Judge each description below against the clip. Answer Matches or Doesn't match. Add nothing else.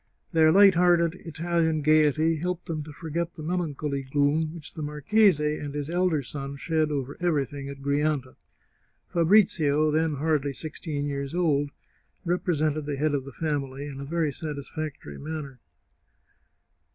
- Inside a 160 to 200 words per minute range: Doesn't match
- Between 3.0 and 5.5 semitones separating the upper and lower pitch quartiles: Doesn't match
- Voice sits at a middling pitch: Matches